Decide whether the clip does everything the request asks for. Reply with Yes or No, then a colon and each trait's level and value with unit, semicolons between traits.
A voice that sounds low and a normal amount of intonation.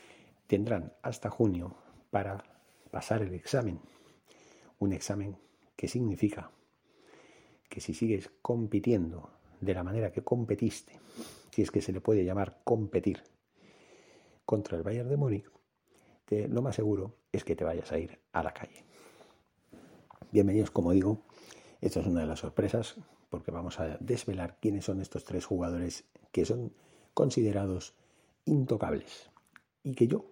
Yes: low, 105 Hz; average, 3.8 semitones